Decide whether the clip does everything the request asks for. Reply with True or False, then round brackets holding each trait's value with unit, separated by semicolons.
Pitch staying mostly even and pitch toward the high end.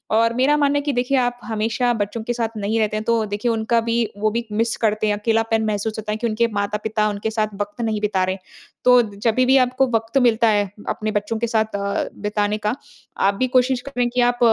True (2.3 semitones; 225 Hz)